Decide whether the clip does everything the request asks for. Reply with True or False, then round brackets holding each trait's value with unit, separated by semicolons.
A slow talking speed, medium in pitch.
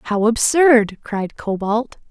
False (115 wpm; 225 Hz)